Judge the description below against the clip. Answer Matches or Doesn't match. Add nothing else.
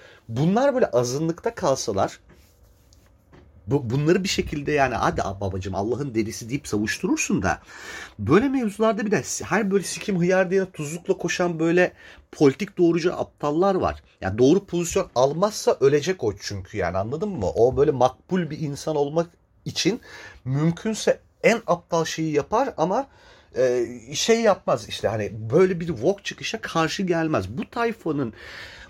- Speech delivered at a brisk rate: Matches